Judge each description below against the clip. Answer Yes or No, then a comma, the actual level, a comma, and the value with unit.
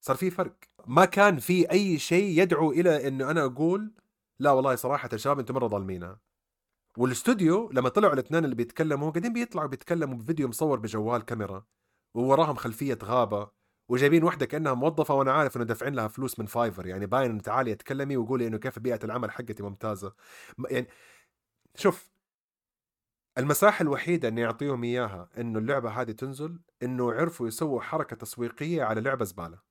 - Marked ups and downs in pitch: Yes, wide, 5.7 semitones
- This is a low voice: Yes, low, 130 Hz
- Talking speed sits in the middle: No, fast, 160 wpm